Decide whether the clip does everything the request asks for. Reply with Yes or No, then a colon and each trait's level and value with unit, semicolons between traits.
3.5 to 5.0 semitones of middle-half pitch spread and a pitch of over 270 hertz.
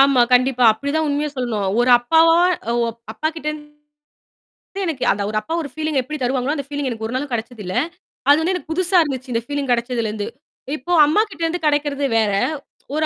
Yes: average, 4.1 semitones; very high, 285 Hz